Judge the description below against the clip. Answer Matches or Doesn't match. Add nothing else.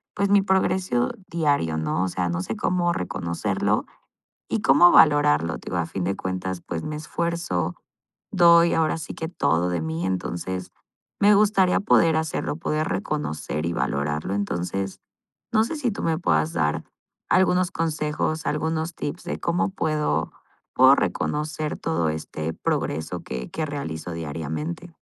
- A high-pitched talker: Doesn't match